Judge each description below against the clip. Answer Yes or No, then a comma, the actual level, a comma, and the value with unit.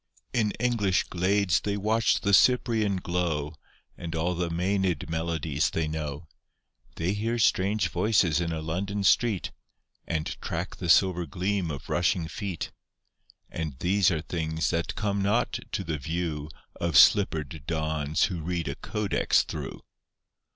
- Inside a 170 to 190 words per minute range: No, average, 145 wpm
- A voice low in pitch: Yes, very low, 90 Hz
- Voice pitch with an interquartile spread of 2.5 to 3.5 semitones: No, average, 3.9 semitones